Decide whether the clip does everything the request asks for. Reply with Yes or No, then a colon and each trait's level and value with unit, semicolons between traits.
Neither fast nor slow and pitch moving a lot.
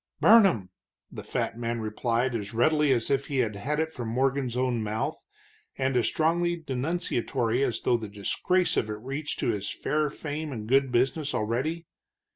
No: average, 175 wpm; average, 4.7 semitones